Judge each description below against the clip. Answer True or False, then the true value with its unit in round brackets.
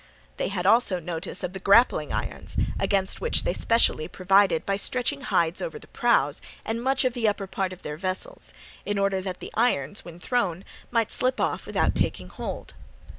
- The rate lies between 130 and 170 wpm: False (185 wpm)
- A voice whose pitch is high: True (195 Hz)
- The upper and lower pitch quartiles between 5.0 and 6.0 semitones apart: False (4.4 semitones)